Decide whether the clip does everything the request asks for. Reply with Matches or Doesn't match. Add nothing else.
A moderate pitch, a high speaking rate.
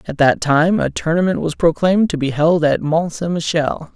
Matches